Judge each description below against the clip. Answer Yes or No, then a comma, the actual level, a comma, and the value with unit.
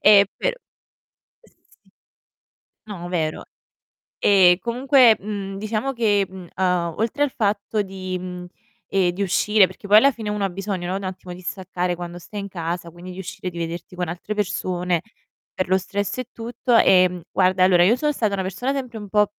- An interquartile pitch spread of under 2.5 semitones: No, average, 2.9 semitones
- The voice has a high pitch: Yes, high, 195 Hz